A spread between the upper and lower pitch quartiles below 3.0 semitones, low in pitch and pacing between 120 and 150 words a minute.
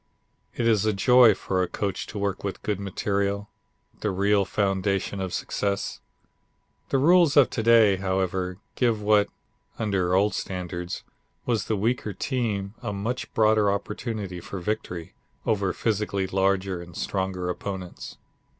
Yes: narrow, 2.4 semitones; low, 100 Hz; average, 140 wpm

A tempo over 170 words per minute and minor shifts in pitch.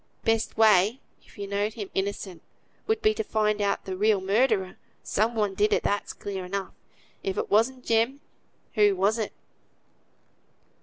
No: average, 160 wpm; narrow, 2.3 semitones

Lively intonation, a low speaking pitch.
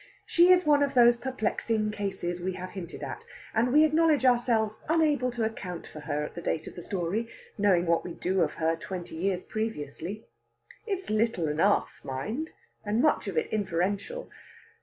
No: wide, 5.9 semitones; high, 210 Hz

